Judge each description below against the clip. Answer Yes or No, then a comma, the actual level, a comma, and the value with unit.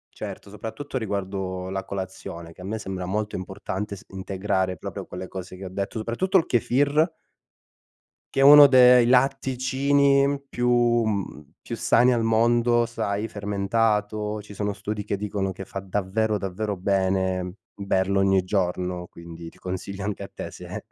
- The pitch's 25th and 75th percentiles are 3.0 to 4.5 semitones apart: Yes, average, 3.8 semitones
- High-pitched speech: No, low, 100 Hz